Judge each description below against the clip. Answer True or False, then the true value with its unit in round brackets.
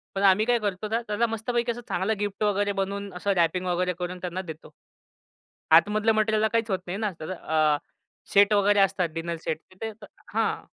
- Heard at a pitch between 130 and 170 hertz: False (200 Hz)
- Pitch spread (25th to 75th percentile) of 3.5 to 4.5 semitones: False (3.0 semitones)